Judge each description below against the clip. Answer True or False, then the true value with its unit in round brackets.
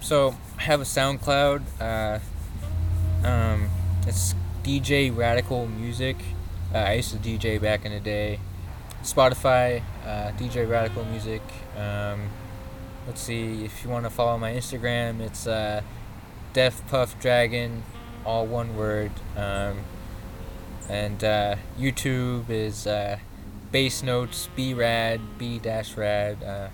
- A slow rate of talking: True (125 wpm)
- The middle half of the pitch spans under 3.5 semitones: True (3.0 semitones)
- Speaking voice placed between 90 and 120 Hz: True (110 Hz)